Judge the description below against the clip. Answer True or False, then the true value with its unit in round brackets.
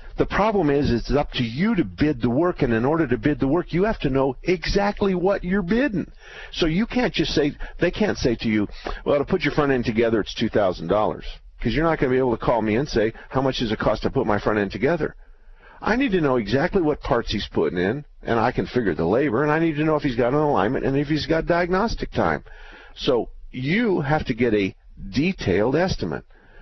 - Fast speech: True (245 wpm)